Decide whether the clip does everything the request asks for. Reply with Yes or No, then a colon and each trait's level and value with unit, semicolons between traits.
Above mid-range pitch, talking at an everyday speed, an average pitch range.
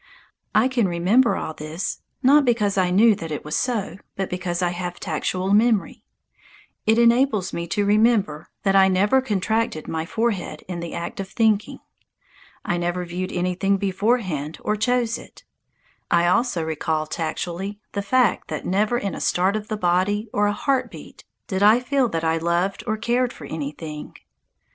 Yes: high, 195 Hz; average, 170 wpm; average, 4.3 semitones